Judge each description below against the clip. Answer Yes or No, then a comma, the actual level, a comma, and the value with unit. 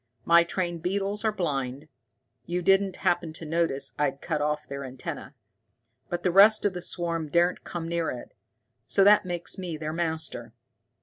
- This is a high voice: No, medium, 170 Hz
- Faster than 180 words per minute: No, average, 170 wpm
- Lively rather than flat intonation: No, average, 3.2 semitones